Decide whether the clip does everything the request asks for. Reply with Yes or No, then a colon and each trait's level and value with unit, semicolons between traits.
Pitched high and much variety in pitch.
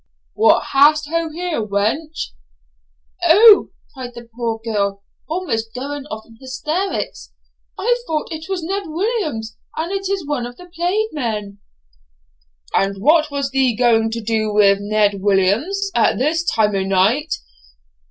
Yes: very high, 270 Hz; wide, 7.3 semitones